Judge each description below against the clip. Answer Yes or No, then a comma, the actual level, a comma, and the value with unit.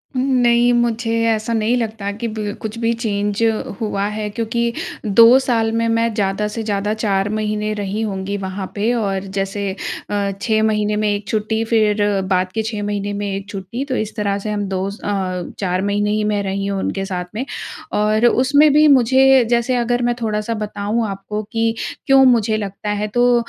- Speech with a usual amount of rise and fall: No, narrow, 2.3 semitones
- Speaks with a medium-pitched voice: No, high, 215 Hz